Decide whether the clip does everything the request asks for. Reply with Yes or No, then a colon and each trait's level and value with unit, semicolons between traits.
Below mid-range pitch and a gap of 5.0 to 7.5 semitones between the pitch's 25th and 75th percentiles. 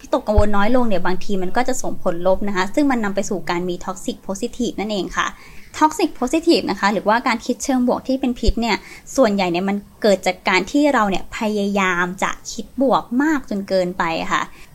No: high, 210 Hz; average, 5.3 semitones